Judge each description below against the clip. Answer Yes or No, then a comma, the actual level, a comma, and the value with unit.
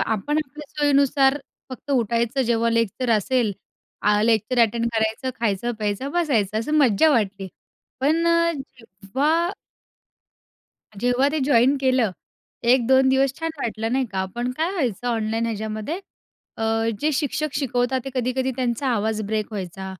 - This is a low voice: No, high, 245 Hz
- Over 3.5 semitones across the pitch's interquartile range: Yes, average, 3.9 semitones